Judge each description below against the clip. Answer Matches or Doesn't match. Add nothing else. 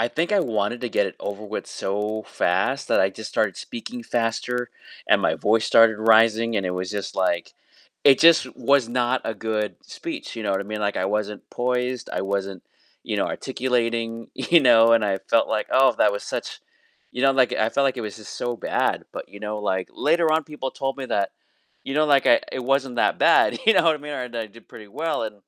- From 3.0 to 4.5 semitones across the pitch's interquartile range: Matches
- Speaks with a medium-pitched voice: Doesn't match